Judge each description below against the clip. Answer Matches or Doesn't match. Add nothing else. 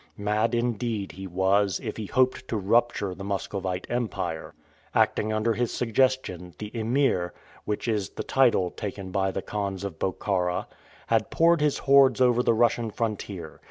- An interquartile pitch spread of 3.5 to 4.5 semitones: Matches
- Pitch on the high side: Doesn't match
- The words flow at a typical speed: Matches